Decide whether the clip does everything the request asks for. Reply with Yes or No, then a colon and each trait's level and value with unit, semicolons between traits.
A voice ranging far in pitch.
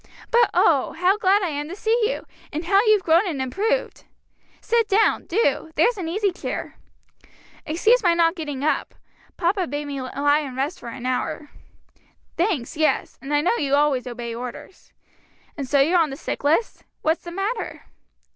Yes: wide, 5.7 semitones